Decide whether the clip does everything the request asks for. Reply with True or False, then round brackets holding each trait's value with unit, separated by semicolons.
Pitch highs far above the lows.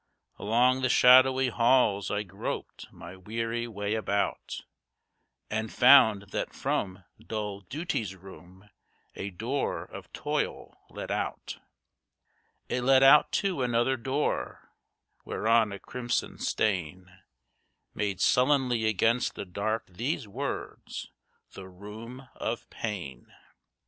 False (4.1 semitones)